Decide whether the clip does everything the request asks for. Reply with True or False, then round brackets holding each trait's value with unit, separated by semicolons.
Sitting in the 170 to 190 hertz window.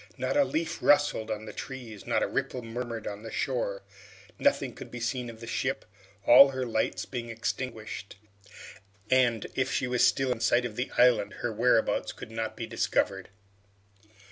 False (120 Hz)